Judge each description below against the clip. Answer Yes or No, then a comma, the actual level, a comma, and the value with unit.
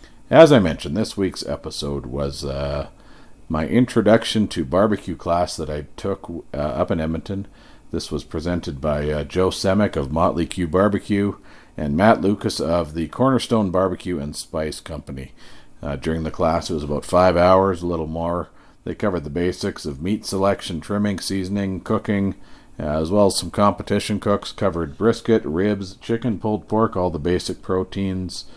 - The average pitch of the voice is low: Yes, very low, 95 Hz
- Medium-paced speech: Yes, average, 170 wpm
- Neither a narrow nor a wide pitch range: Yes, average, 4.1 semitones